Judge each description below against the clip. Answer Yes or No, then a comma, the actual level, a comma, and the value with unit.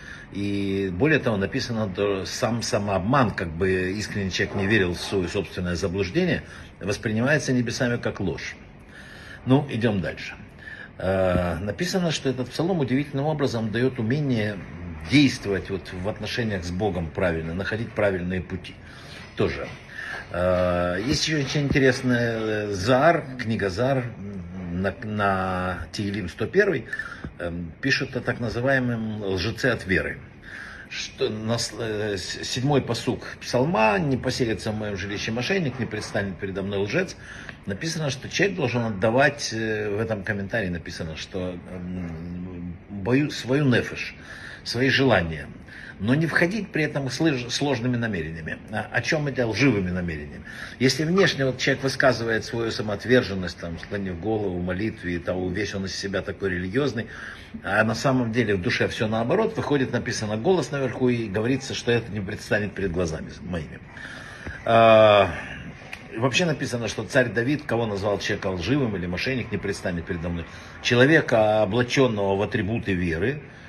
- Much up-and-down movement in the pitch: No, average, 5.0 semitones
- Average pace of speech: Yes, average, 135 wpm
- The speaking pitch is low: Yes, low, 110 Hz